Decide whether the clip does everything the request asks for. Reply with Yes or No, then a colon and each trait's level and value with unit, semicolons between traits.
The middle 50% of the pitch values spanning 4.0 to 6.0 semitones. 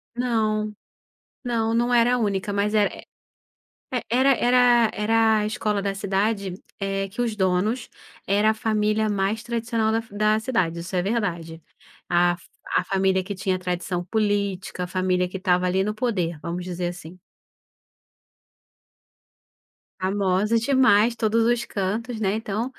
No: average, 3.2 semitones